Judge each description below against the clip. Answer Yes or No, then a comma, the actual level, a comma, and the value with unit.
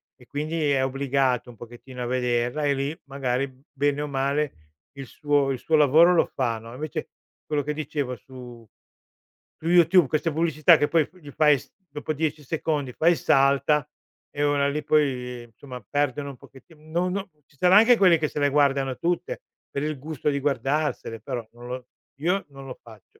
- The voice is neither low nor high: Yes, medium, 145 Hz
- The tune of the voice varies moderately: Yes, average, 3.0 semitones